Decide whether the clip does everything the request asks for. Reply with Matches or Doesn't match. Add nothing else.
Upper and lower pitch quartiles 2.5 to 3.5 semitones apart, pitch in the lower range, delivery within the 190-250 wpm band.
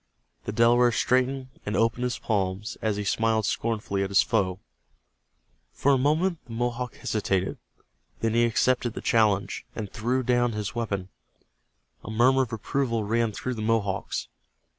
Doesn't match